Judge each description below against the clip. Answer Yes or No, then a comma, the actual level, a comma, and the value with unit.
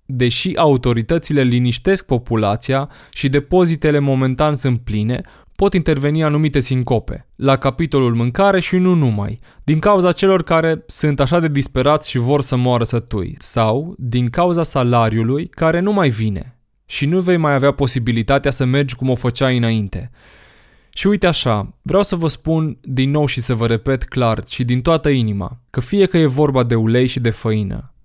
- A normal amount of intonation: Yes, average, 4.5 semitones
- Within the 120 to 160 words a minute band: No, fast, 170 wpm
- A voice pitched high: No, low, 135 Hz